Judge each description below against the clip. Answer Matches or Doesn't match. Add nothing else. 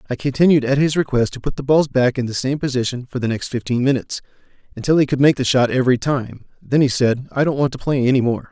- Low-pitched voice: Matches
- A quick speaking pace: Matches